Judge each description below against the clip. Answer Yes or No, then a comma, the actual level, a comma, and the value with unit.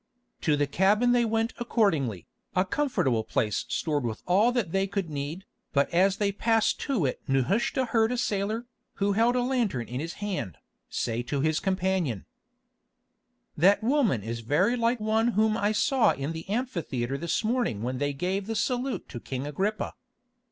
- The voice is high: Yes, high, 195 Hz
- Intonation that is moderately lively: No, wide, 8.0 semitones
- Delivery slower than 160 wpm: No, average, 175 wpm